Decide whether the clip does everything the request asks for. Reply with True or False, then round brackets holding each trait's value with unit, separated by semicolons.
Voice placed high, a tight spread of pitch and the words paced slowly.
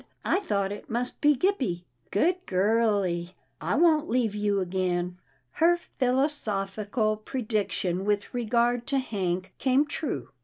False (215 Hz; 5.3 semitones; 125 wpm)